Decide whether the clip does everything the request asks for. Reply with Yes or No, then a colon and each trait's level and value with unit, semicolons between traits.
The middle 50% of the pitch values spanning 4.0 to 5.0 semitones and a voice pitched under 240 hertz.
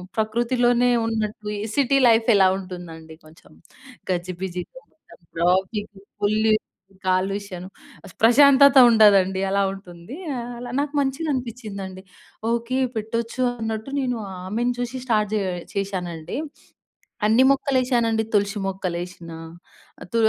Yes: average, 4.5 semitones; high, 215 Hz